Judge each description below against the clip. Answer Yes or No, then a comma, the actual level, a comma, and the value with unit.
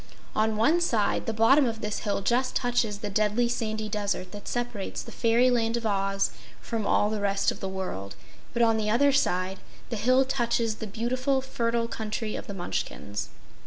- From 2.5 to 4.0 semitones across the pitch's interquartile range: Yes, average, 2.8 semitones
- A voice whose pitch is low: No, high, 220 Hz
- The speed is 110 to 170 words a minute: No, average, 185 wpm